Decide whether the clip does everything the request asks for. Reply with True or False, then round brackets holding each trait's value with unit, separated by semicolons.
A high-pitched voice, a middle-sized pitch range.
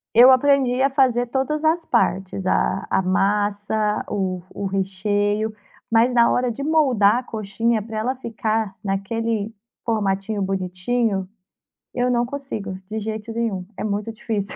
True (220 Hz; 3.6 semitones)